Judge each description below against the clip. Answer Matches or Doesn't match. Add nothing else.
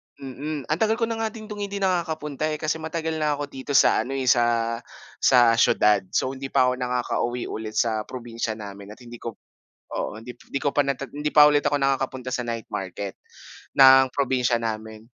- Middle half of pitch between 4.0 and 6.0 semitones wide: Matches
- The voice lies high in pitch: Doesn't match